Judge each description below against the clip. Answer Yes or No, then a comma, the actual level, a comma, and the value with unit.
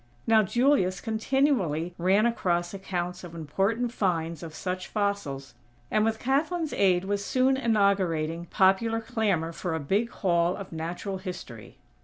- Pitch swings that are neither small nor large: Yes, average, 4.6 semitones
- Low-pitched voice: No, high, 190 Hz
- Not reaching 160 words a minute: Yes, average, 140 wpm